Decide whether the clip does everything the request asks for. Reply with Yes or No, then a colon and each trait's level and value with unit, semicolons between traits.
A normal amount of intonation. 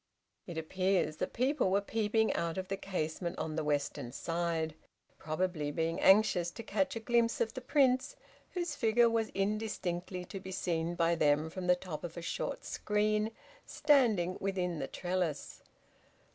Yes: average, 4.6 semitones